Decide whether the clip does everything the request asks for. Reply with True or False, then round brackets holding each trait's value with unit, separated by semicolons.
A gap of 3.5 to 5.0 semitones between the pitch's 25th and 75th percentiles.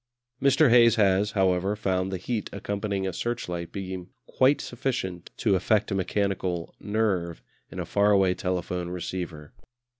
False (2.9 semitones)